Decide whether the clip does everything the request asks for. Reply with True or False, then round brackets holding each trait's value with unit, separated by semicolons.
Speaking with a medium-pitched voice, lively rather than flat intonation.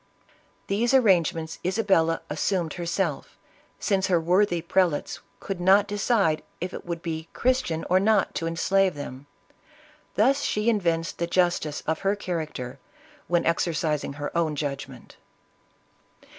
False (175 Hz; 3.4 semitones)